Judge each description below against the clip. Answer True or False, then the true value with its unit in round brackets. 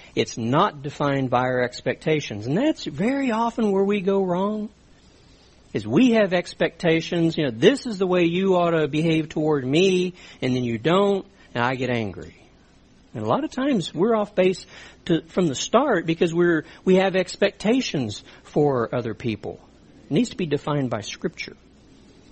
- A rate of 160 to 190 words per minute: True (175 wpm)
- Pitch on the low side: False (170 Hz)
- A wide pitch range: True (6.4 semitones)